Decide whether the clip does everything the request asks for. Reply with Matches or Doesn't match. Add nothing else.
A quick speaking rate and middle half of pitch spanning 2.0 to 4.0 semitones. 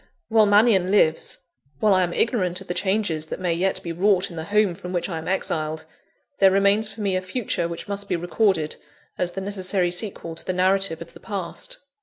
Matches